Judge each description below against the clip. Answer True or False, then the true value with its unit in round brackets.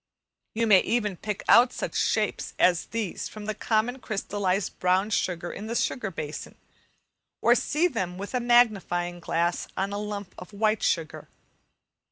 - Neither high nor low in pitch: False (205 Hz)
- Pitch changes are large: False (3.6 semitones)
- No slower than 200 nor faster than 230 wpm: False (160 wpm)